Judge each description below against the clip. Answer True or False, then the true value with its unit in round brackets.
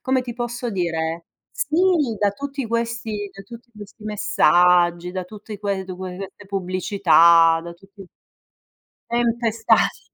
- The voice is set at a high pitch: True (200 Hz)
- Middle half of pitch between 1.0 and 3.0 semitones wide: False (4.5 semitones)